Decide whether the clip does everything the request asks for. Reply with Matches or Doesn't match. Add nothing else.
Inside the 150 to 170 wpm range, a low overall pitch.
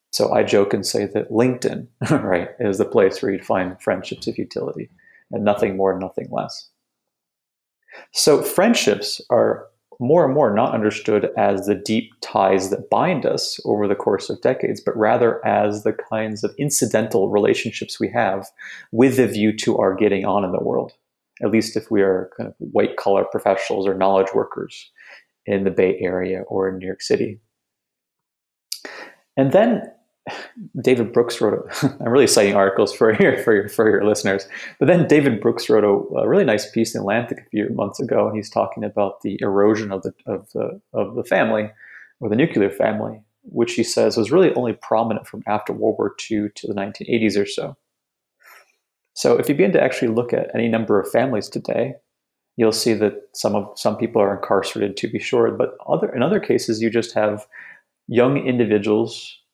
Doesn't match